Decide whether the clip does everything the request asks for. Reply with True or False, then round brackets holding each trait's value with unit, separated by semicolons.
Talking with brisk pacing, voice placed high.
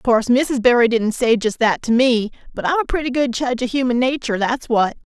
True (245 wpm; 245 Hz)